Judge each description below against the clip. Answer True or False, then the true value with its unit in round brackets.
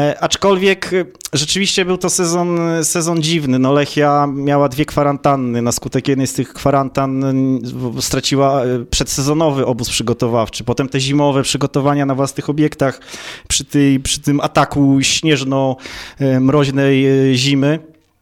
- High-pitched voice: False (140 Hz)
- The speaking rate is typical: True (120 wpm)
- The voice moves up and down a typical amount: False (2.0 semitones)